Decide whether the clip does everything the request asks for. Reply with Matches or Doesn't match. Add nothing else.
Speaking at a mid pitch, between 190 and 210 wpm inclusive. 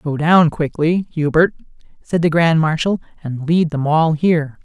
Doesn't match